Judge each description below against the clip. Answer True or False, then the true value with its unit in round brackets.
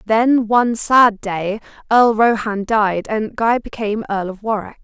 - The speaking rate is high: False (160 wpm)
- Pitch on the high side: True (215 Hz)